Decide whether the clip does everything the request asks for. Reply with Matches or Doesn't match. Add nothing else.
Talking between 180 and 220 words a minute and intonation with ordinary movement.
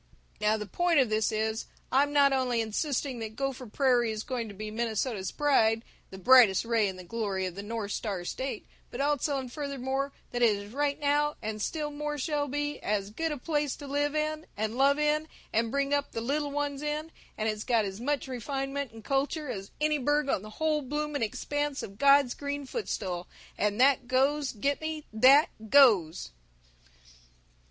Matches